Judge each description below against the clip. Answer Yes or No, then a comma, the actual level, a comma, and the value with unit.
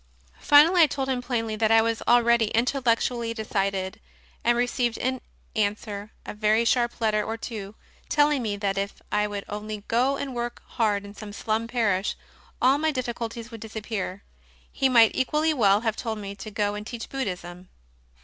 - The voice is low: No, high, 225 Hz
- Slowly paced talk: No, average, 175 wpm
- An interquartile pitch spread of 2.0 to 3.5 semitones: Yes, average, 2.8 semitones